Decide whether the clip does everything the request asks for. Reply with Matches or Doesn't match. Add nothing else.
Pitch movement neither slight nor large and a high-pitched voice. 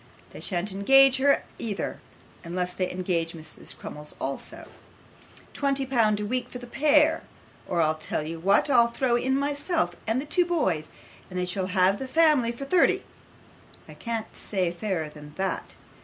Doesn't match